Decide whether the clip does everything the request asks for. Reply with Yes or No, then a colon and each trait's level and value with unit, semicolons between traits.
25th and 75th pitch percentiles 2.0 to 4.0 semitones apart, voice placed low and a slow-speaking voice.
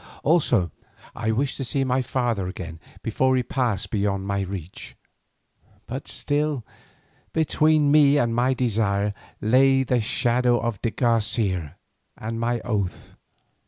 No: average, 4.6 semitones; low, 120 Hz; slow, 130 wpm